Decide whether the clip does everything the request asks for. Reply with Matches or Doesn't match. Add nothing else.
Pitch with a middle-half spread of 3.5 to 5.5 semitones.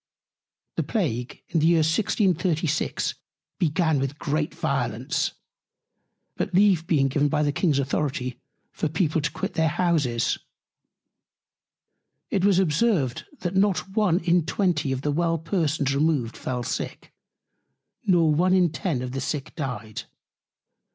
Matches